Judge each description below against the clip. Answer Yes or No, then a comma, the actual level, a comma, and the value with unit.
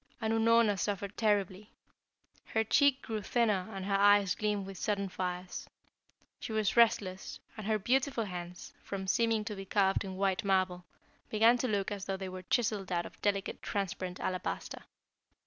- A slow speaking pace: No, average, 165 wpm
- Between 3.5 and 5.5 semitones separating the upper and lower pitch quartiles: No, narrow, 2.6 semitones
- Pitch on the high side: Yes, high, 200 Hz